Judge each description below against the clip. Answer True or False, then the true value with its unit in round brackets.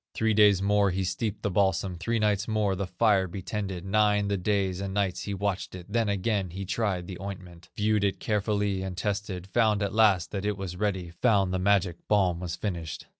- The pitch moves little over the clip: True (2.0 semitones)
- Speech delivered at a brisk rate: True (210 wpm)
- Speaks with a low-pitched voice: True (100 Hz)